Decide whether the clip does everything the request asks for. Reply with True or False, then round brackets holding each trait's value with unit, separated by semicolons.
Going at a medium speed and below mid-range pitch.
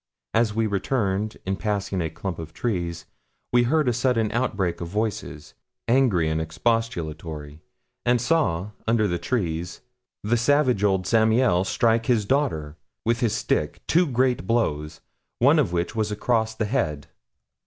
True (150 wpm; 105 Hz)